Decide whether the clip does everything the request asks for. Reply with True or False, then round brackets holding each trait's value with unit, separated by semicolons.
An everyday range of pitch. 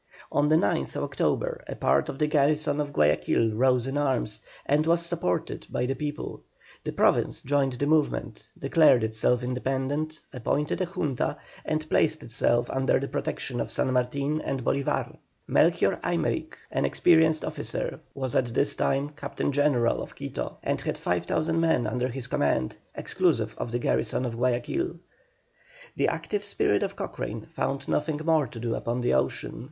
True (3.9 semitones)